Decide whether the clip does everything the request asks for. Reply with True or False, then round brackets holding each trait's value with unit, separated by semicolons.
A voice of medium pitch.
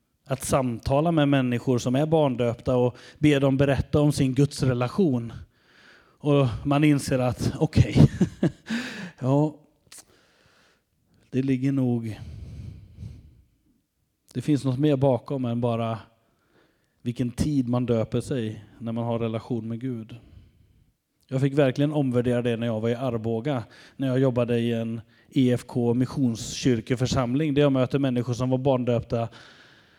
False (125 Hz)